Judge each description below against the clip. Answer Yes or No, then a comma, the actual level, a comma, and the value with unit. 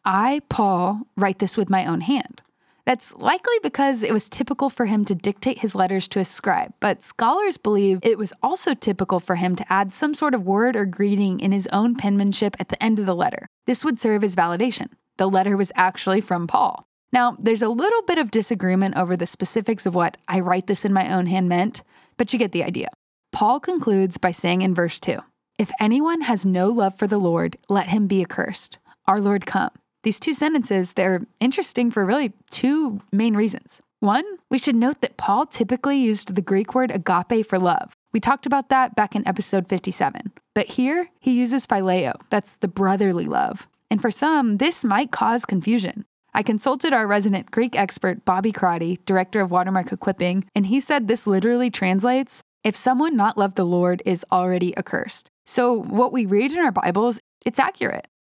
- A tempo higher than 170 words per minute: Yes, average, 200 wpm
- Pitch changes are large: No, average, 4.6 semitones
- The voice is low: No, high, 210 Hz